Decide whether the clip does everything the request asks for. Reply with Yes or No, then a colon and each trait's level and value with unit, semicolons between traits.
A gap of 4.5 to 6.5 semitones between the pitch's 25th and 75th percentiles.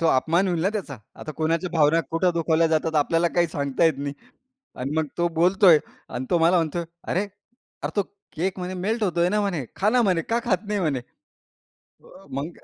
No: average, 2.7 semitones